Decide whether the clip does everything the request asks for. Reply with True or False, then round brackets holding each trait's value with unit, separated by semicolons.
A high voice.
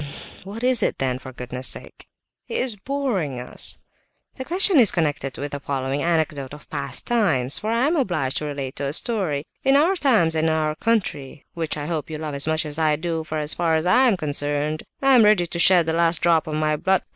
False (160 Hz)